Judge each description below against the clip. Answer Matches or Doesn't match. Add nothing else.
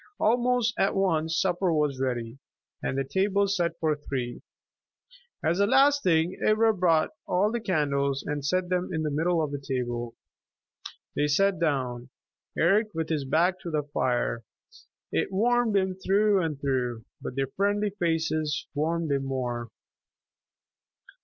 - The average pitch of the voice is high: Doesn't match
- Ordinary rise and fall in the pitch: Doesn't match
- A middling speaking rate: Matches